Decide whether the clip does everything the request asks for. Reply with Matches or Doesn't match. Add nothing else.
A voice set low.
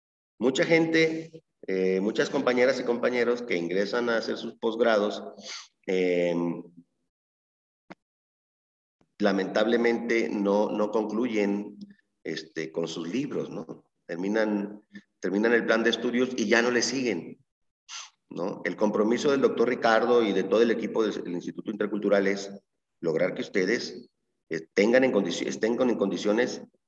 Matches